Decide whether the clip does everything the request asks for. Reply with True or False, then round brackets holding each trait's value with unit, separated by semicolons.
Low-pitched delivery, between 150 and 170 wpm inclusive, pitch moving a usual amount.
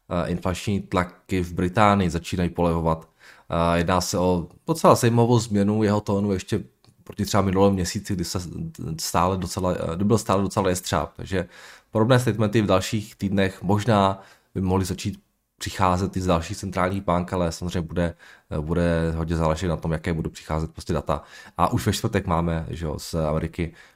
True (95 Hz; 165 wpm; 3.0 semitones)